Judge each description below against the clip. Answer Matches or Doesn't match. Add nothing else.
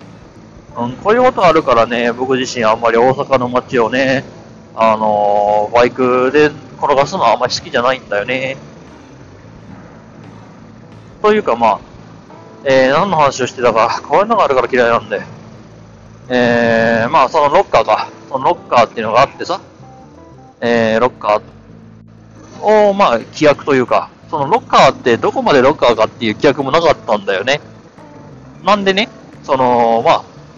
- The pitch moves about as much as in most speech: Matches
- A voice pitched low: Matches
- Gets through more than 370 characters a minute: Doesn't match